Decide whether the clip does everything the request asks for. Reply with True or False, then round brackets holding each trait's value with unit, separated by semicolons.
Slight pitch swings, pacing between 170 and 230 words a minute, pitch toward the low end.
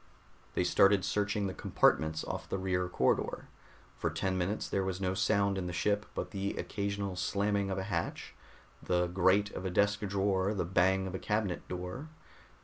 True (1.7 semitones; 180 wpm; 95 Hz)